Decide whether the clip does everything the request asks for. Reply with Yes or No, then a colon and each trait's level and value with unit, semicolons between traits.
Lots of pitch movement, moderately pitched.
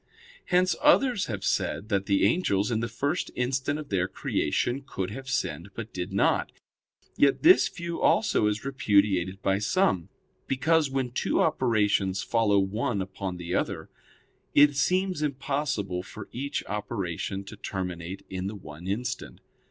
No: wide, 6.2 semitones; low, 105 Hz